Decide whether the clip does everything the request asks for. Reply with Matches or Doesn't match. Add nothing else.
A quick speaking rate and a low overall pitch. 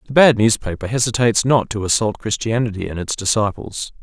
Doesn't match